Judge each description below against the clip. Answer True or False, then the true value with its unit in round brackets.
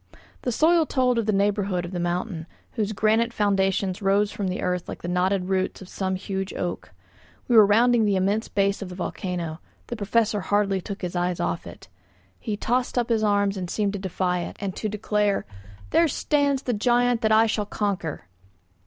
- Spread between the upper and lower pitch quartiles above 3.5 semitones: False (3.0 semitones)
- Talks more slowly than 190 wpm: False (195 wpm)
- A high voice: True (200 Hz)